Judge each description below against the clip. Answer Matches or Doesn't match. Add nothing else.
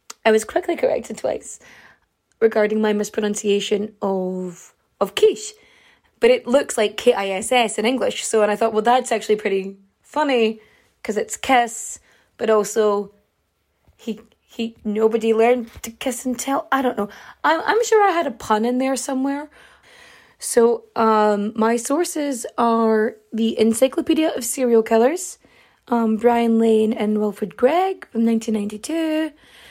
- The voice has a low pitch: Doesn't match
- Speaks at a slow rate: Doesn't match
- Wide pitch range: Doesn't match